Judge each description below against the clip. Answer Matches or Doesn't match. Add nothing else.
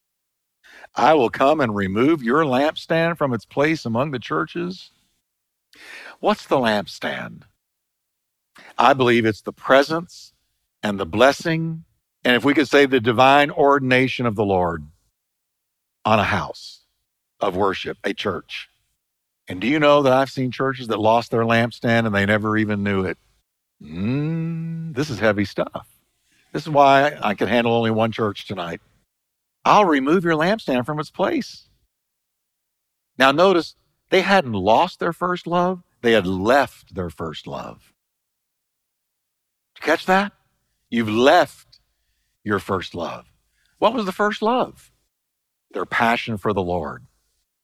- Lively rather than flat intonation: Matches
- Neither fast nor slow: Matches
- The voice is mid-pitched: Doesn't match